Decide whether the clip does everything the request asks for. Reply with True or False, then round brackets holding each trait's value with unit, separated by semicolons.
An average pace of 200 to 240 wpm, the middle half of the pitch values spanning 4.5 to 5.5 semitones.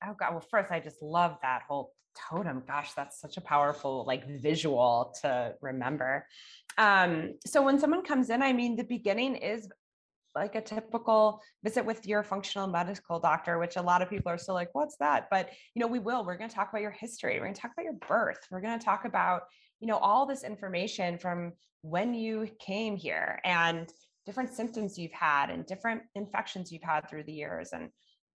True (205 wpm; 5.2 semitones)